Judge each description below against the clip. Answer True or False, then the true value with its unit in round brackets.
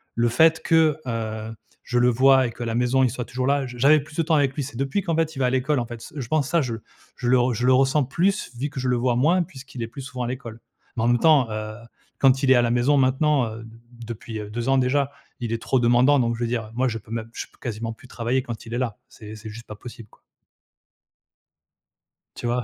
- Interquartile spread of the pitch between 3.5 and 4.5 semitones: False (2.8 semitones)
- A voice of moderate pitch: False (125 Hz)